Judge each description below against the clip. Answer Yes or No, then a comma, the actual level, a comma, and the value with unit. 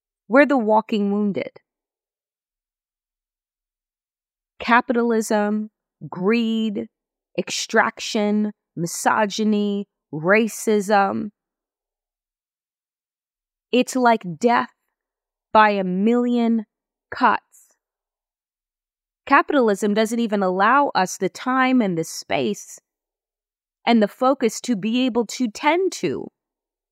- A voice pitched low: No, high, 220 Hz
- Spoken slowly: Yes, slow, 80 wpm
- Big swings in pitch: No, average, 3.2 semitones